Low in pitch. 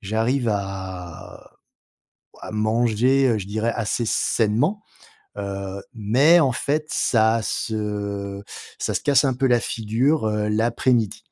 Yes: low, 110 Hz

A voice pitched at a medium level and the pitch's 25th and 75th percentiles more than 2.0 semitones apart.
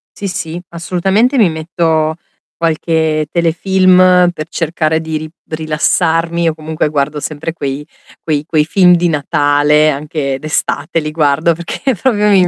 Yes: medium, 160 Hz; narrow, 2.4 semitones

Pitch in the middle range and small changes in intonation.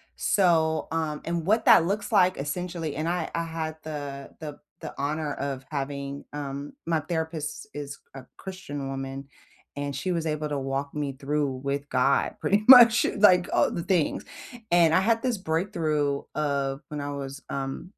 No: medium, 150 Hz; average, 3.3 semitones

